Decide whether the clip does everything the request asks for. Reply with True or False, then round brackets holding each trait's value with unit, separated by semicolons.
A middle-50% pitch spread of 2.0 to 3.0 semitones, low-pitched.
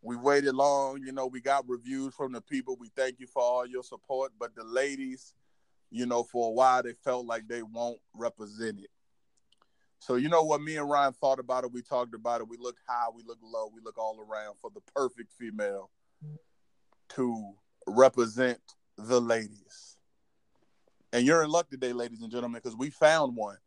True (2.5 semitones; 125 Hz)